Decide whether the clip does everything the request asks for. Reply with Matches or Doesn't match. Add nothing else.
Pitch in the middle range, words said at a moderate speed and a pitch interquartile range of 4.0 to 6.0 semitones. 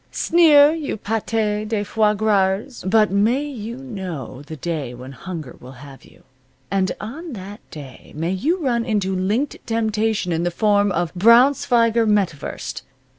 Doesn't match